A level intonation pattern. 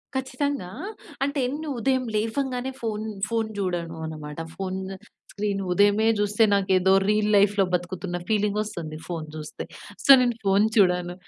No: average, 4.2 semitones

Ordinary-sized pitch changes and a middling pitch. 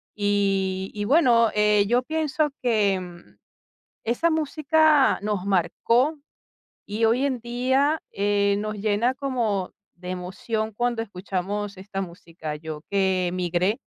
No: average, 4.6 semitones; high, 210 Hz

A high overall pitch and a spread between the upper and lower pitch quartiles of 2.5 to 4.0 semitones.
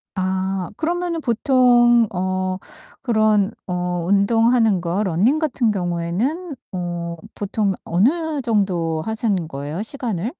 No: high, 205 Hz; average, 5.2 semitones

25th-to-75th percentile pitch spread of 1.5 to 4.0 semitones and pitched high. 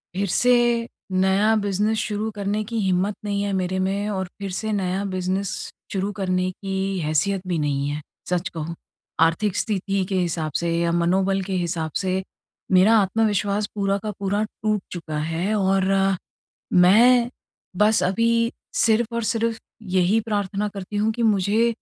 Yes: narrow, 2.4 semitones; high, 195 Hz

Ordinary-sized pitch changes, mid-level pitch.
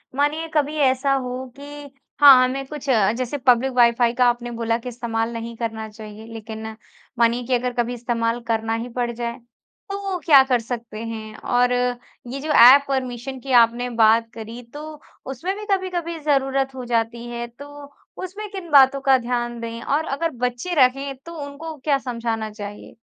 No: average, 3.4 semitones; very high, 250 Hz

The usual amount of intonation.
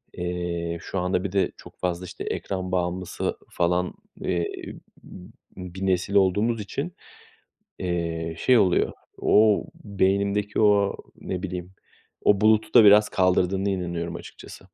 No: narrow, 2.3 semitones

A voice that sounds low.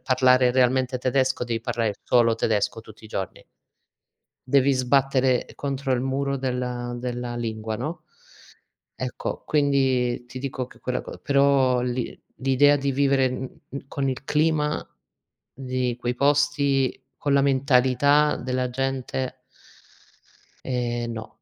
Yes: low, 130 Hz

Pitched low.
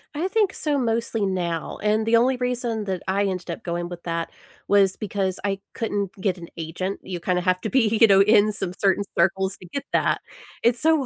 No: high, 200 Hz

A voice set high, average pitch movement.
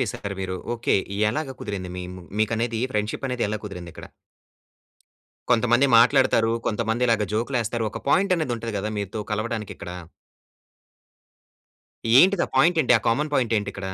No: low, 115 Hz; average, 3.1 semitones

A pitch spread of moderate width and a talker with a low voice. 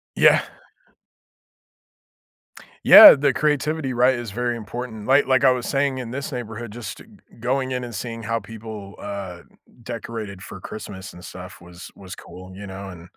Yes: average, 4.3 semitones; low, 115 Hz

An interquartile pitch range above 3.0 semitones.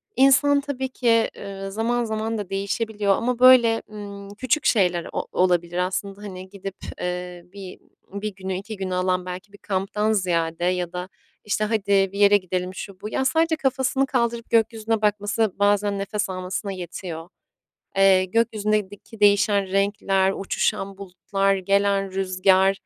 No: average, 2.7 semitones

